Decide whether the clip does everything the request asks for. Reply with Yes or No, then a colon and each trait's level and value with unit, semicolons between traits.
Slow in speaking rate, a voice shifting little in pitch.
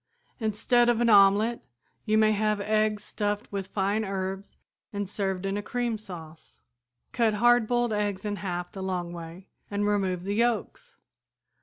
No: average, 155 wpm; narrow, 2.2 semitones